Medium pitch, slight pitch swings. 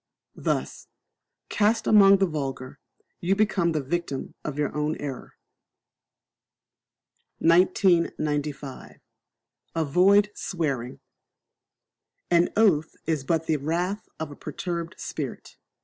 No: medium, 165 Hz; average, 4.2 semitones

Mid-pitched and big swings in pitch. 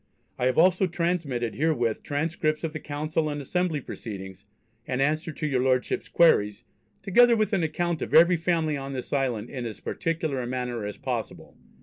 No: medium, 150 Hz; average, 4.7 semitones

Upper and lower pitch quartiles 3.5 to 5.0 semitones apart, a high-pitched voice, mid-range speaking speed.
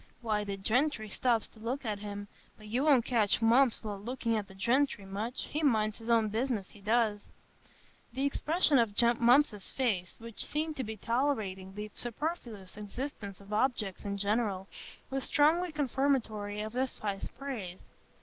Yes: average, 4.3 semitones; high, 225 Hz; average, 160 wpm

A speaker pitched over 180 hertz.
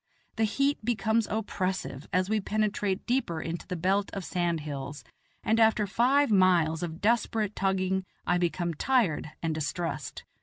Yes: high, 190 Hz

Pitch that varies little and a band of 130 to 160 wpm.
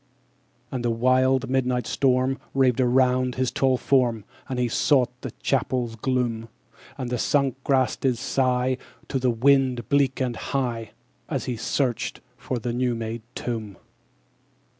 Yes: narrow, 1.6 semitones; average, 155 wpm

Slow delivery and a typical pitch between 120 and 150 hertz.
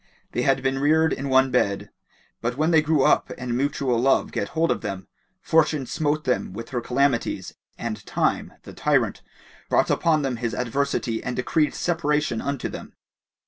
No: average, 175 wpm; low, 135 Hz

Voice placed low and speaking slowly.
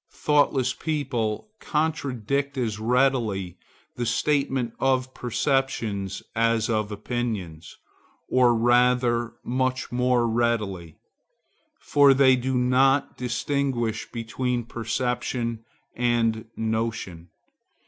Yes: low, 120 Hz; slow, 85 wpm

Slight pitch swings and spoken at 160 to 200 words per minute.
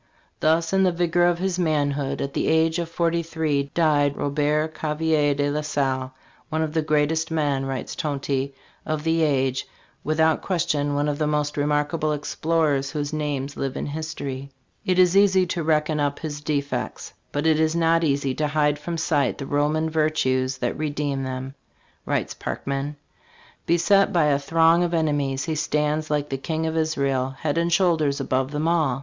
Yes: narrow, 2.2 semitones; average, 180 wpm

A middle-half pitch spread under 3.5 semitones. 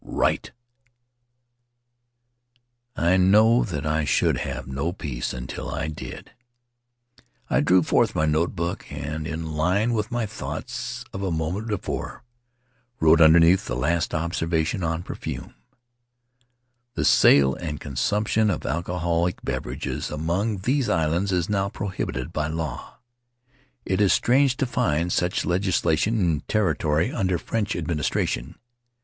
No: average, 4.1 semitones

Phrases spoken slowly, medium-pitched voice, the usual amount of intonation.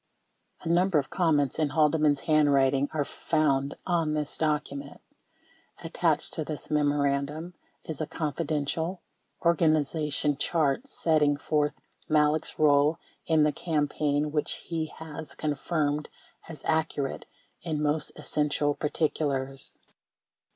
No: slow, 115 wpm; medium, 150 Hz; narrow, 1.6 semitones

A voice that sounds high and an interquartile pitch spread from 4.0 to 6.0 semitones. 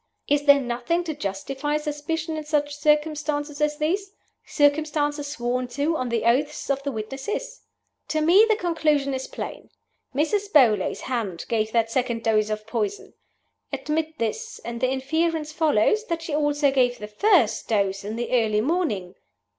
Yes: very high, 285 Hz; average, 4.7 semitones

